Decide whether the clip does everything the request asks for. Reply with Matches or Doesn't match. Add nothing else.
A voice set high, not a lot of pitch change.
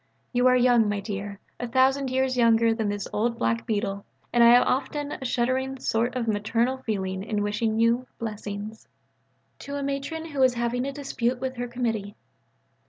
Doesn't match